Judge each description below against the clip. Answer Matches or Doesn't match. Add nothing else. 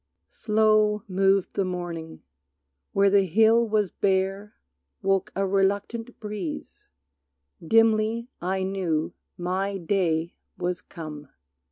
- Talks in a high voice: Matches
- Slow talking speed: Matches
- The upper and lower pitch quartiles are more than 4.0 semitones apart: Doesn't match